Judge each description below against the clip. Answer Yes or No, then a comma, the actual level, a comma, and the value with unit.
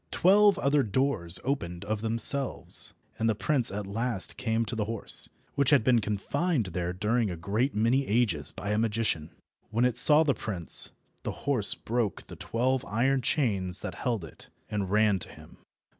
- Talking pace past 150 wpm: Yes, average, 175 wpm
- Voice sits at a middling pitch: No, low, 115 Hz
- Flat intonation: No, average, 4.3 semitones